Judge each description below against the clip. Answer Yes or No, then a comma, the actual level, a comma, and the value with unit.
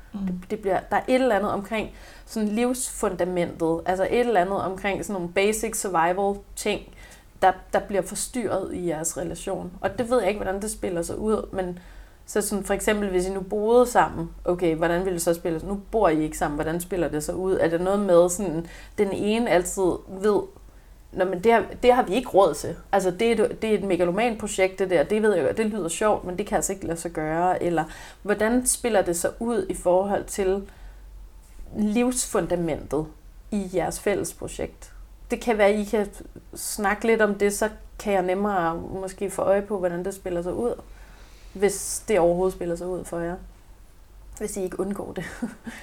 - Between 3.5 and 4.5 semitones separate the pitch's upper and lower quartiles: No, average, 3.1 semitones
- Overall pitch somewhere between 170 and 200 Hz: Yes, high, 190 Hz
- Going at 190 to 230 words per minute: Yes, average, 205 wpm